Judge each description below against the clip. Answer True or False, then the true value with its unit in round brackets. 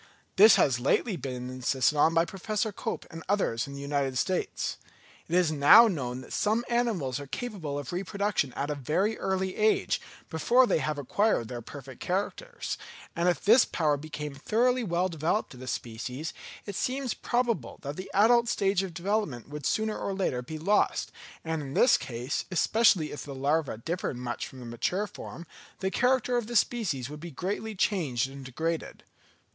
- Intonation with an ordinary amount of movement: False (7.1 semitones)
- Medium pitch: True (165 Hz)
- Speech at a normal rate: True (180 wpm)